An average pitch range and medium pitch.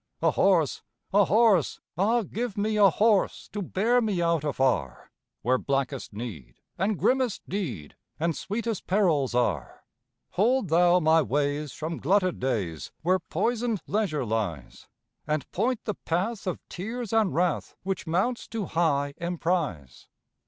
No: wide, 6.7 semitones; medium, 175 Hz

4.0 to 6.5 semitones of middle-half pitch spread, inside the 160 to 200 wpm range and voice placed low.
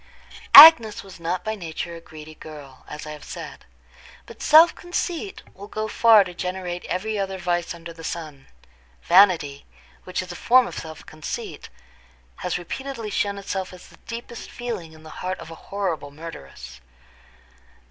No: average, 4.7 semitones; average, 165 wpm; medium, 180 Hz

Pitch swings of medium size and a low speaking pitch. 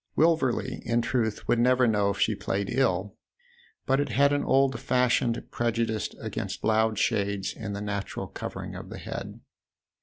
Yes: average, 3.8 semitones; low, 115 Hz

